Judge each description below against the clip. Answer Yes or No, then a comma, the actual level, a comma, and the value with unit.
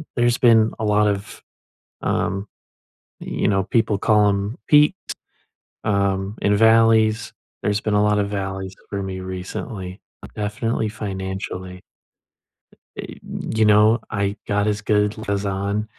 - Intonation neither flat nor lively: No, narrow, 1.8 semitones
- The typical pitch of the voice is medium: No, low, 105 Hz